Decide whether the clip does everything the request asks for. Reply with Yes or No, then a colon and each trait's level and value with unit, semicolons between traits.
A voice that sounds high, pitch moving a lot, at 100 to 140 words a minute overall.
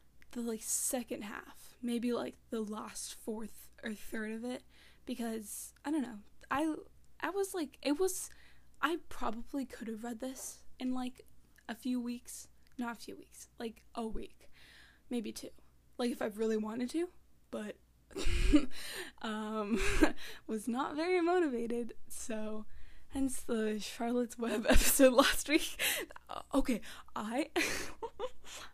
No: high, 245 Hz; average, 4.2 semitones; slow, 135 wpm